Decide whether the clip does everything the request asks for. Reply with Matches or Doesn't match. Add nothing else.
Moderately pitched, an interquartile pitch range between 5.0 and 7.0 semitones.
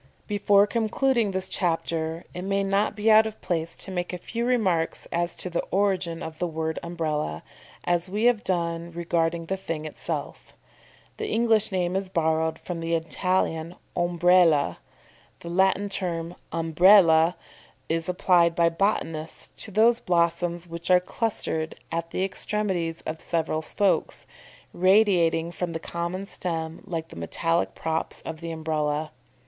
Doesn't match